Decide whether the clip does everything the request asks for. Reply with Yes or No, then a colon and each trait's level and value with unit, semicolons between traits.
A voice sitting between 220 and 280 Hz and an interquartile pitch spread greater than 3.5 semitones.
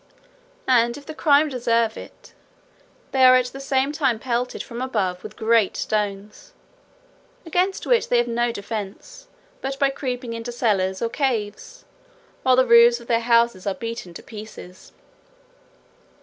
No: high, 235 Hz; average, 3.1 semitones